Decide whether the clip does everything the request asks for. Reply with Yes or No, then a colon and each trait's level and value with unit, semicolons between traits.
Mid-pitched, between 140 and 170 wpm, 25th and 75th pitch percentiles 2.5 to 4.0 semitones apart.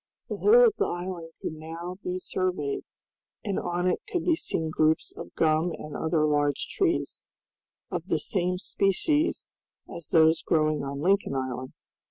Yes: medium, 170 Hz; average, 160 wpm; average, 3.2 semitones